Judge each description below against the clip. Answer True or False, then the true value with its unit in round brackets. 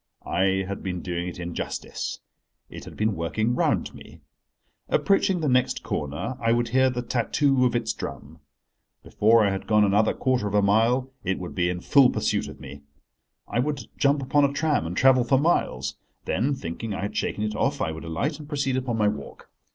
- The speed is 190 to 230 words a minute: True (200 wpm)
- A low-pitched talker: True (115 Hz)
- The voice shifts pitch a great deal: True (5.7 semitones)